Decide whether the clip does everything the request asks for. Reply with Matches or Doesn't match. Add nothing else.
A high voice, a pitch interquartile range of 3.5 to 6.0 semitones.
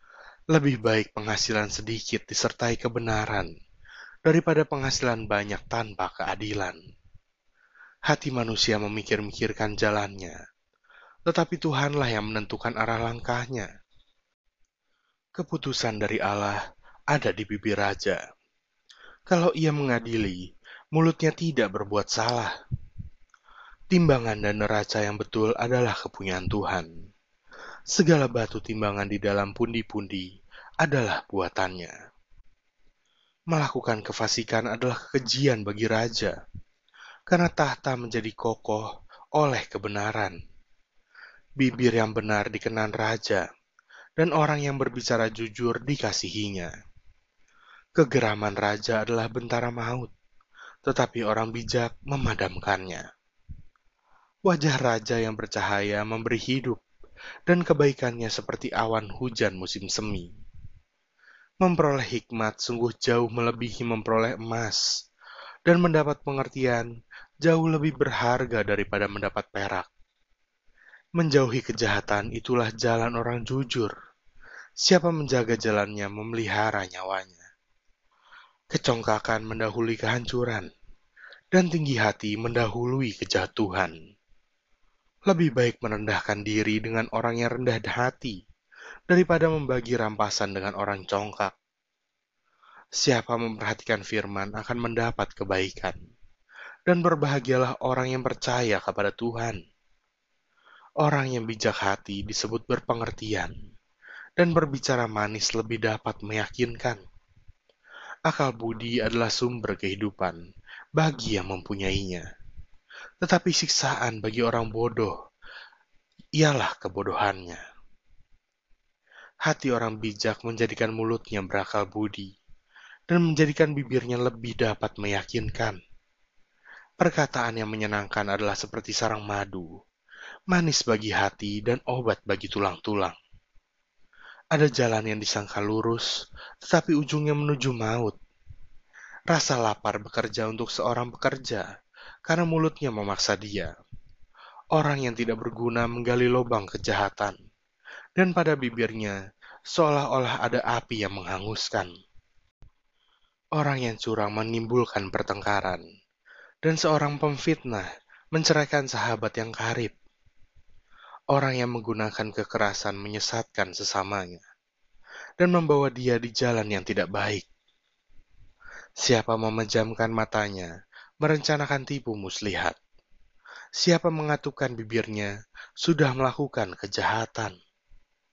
Doesn't match